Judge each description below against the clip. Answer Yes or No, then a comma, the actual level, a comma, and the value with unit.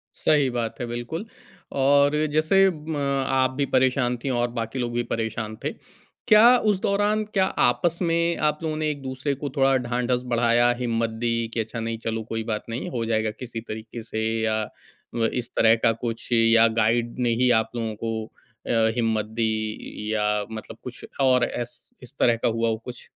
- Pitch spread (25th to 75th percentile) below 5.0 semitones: Yes, average, 3.0 semitones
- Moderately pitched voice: No, low, 120 Hz